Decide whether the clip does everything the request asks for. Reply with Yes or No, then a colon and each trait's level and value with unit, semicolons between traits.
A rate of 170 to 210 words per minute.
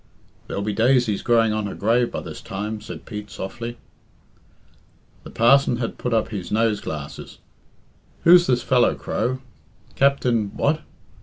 No: average, 145 wpm